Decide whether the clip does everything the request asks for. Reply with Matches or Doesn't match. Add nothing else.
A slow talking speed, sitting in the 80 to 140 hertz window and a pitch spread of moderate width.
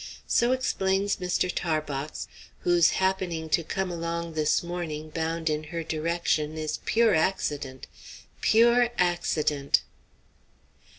Doesn't match